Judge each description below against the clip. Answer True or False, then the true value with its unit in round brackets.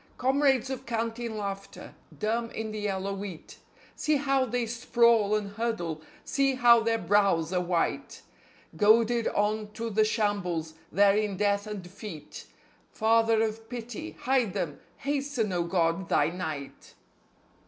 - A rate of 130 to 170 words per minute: True (140 wpm)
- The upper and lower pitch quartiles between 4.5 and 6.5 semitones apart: False (3.2 semitones)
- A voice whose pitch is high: True (215 Hz)